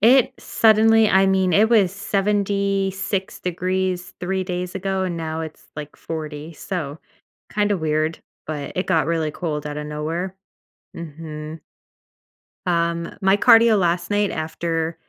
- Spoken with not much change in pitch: No, average, 3.6 semitones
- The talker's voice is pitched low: No, medium, 180 Hz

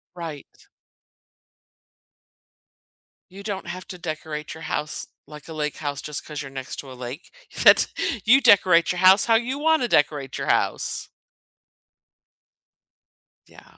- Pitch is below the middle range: No, medium, 160 Hz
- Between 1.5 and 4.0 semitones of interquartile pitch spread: No, average, 4.6 semitones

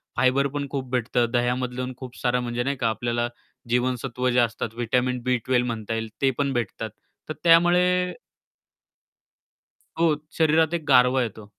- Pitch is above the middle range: No, low, 125 Hz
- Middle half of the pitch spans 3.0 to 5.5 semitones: No, narrow, 2.5 semitones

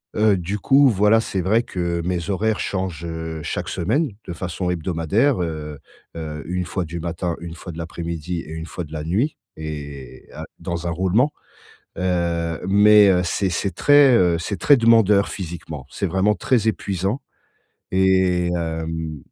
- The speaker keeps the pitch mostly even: No, average, 3.7 semitones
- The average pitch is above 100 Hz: No, very low, 90 Hz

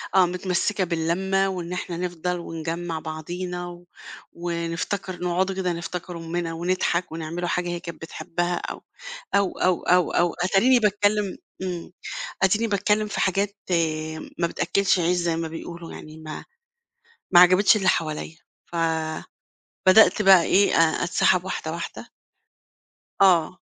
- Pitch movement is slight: Yes, narrow, 2.0 semitones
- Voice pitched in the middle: Yes, medium, 175 Hz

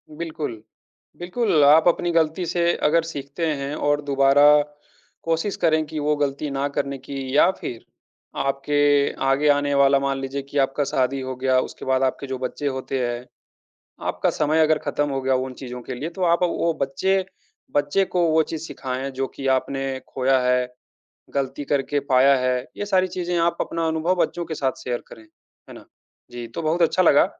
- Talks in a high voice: No, medium, 145 Hz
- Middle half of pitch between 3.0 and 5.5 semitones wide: Yes, average, 3.3 semitones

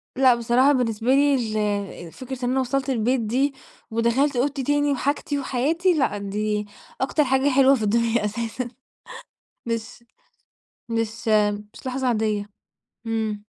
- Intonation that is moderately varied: Yes, average, 3.2 semitones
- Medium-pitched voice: No, very high, 250 Hz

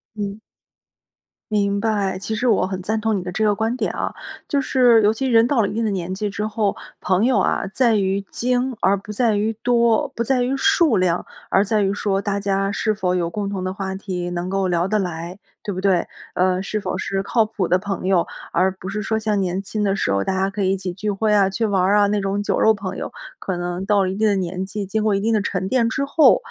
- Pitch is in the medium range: No, high, 200 Hz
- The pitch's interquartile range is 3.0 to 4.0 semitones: No, narrow, 2.4 semitones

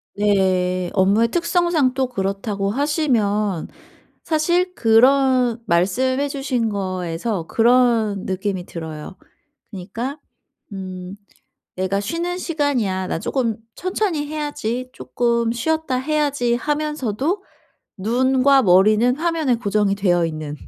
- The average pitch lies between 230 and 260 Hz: Yes, high, 235 Hz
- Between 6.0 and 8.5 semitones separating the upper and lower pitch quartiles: Yes, wide, 6.6 semitones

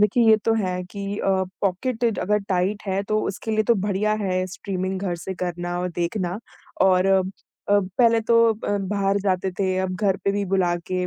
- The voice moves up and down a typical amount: No, narrow, 2.2 semitones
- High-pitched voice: Yes, high, 195 Hz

